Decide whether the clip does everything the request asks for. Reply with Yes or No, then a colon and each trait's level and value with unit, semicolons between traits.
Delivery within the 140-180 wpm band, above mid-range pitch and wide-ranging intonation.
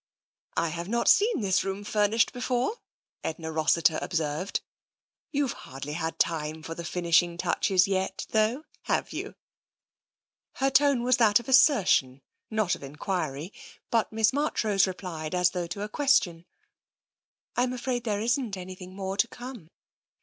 Yes: average, 155 wpm; high, 195 Hz; wide, 6.0 semitones